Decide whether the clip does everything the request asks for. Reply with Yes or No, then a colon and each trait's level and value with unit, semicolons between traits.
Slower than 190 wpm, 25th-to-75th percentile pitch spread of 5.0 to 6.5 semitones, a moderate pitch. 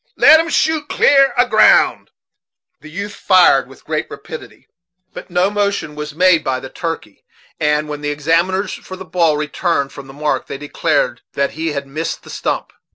No: average, 180 wpm; average, 4.5 semitones; medium, 165 Hz